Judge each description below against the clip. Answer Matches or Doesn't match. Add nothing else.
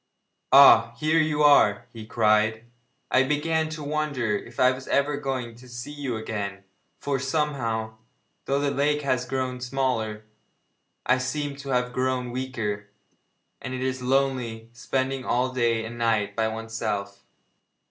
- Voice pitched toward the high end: Doesn't match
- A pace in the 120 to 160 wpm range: Matches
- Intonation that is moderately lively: Matches